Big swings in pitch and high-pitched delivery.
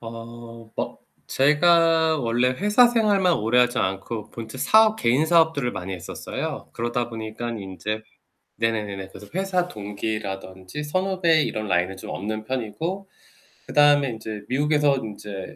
No: wide, 6.8 semitones; low, 120 Hz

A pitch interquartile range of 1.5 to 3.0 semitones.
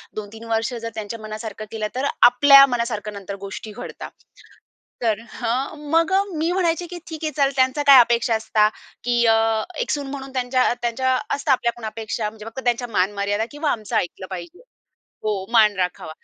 No: average, 4.0 semitones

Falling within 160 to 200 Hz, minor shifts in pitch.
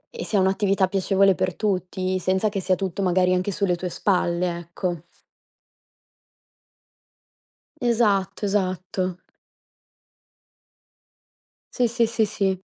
Yes: high, 190 Hz; narrow, 1.7 semitones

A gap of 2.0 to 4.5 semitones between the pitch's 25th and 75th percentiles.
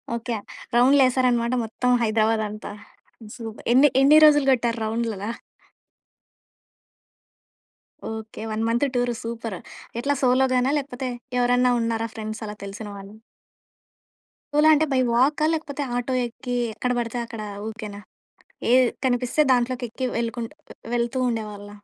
Yes: narrow, 2.5 semitones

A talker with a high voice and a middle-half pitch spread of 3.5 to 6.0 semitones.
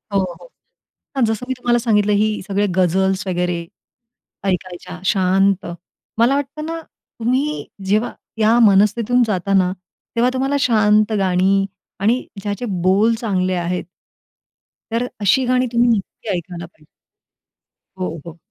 Yes: high, 205 Hz; average, 4.2 semitones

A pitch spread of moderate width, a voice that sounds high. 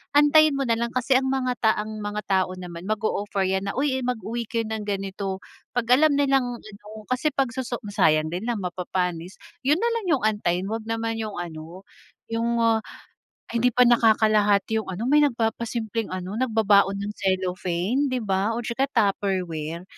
Yes: average, 4.2 semitones; high, 220 Hz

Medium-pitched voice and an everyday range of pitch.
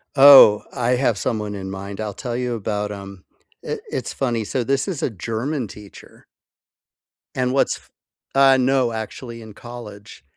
No: low, 115 Hz; average, 3.8 semitones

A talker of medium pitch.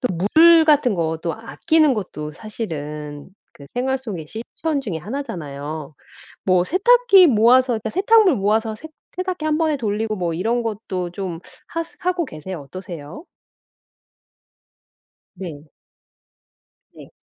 No: high, 215 Hz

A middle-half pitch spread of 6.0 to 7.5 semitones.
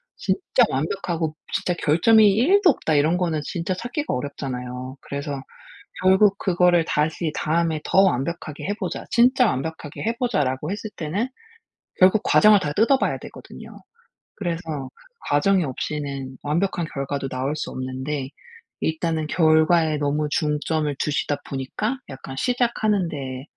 No: average, 5.1 semitones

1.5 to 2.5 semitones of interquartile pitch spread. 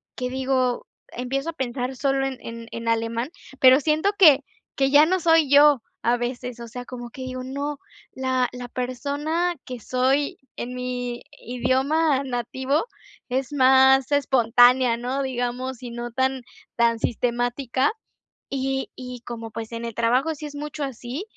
Yes: narrow, 2.2 semitones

